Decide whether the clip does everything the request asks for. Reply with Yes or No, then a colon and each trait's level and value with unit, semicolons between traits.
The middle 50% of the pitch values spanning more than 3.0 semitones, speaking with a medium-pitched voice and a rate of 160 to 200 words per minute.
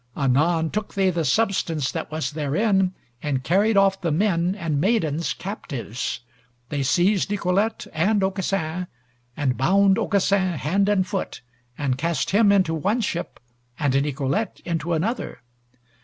No: average, 4.9 semitones; medium, 175 Hz; average, 140 wpm